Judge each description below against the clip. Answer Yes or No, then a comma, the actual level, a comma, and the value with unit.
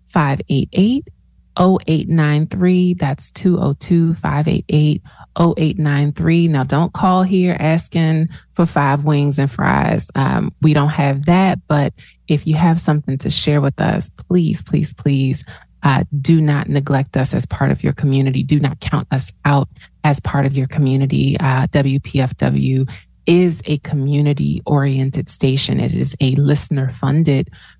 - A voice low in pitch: No, medium, 150 Hz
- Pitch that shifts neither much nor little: Yes, average, 3.2 semitones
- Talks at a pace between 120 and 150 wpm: Yes, average, 140 wpm